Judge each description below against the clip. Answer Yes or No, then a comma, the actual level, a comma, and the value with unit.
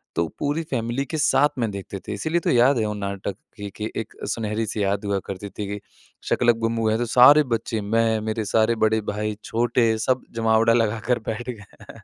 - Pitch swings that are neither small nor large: No, narrow, 2.3 semitones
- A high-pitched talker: No, low, 110 Hz